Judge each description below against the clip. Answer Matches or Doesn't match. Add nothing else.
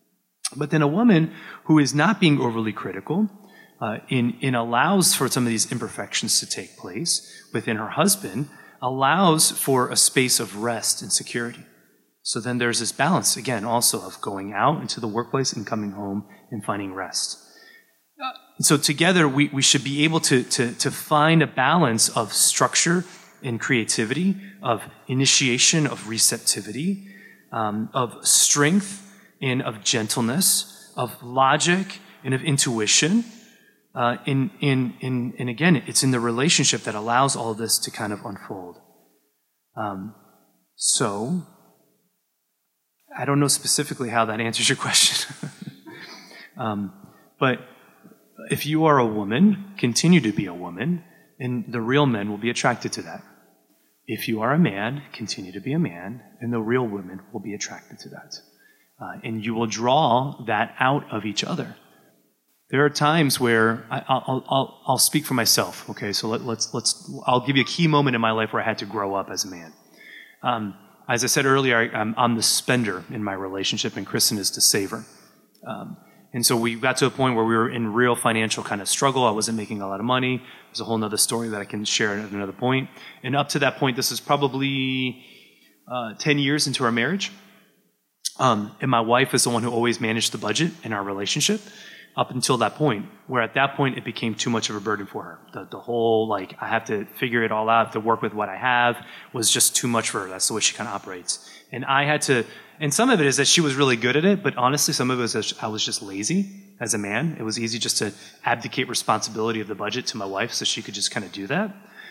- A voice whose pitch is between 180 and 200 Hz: Doesn't match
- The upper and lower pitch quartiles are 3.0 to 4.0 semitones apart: Doesn't match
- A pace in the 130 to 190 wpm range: Doesn't match